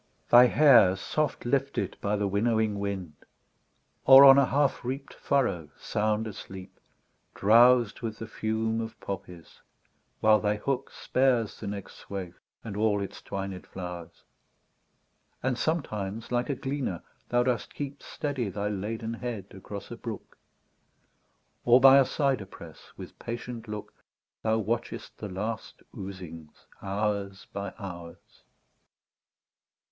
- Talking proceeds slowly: Yes, slow, 130 wpm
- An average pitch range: Yes, average, 3.9 semitones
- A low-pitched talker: Yes, low, 110 Hz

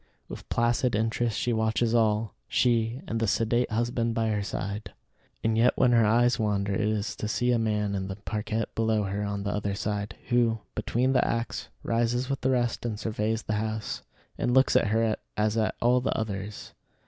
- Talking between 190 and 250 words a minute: Yes, average, 195 wpm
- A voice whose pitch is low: Yes, low, 110 Hz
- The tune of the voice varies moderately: No, narrow, 2.0 semitones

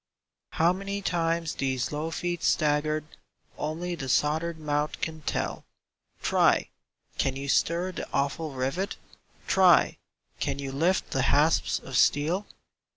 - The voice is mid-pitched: Yes, medium, 155 Hz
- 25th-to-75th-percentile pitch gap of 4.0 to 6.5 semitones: No, average, 3.5 semitones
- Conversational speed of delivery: No, slow, 130 wpm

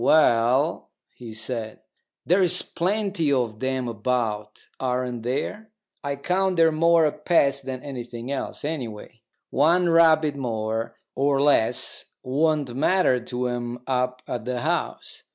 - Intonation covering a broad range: No, average, 4.6 semitones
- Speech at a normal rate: No, slow, 130 wpm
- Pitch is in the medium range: No, low, 130 Hz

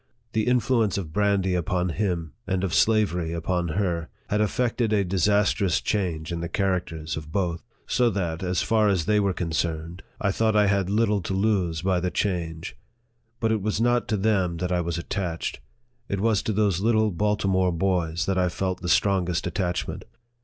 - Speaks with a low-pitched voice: Yes, very low, 95 Hz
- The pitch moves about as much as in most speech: Yes, average, 3.4 semitones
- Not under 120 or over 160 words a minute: No, average, 185 wpm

